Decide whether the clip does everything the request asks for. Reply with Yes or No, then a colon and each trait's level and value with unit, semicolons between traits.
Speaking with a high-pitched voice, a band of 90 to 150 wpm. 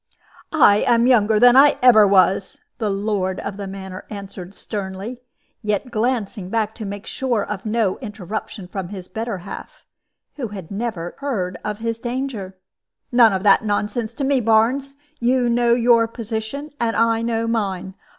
No: high, 220 Hz; average, 165 wpm